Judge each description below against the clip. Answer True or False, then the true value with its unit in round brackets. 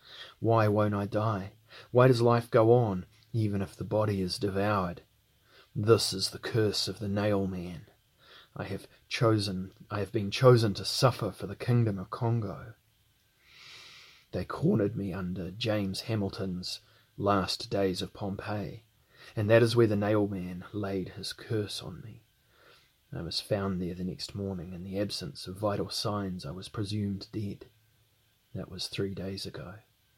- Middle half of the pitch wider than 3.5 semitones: False (2.5 semitones)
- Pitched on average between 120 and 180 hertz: False (105 Hz)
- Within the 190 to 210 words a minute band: False (160 wpm)